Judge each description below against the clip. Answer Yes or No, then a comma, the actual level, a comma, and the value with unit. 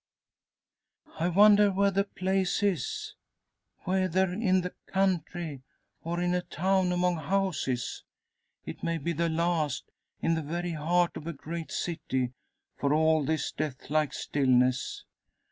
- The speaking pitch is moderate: Yes, medium, 170 Hz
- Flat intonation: No, average, 3.3 semitones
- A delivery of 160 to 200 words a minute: No, slow, 135 wpm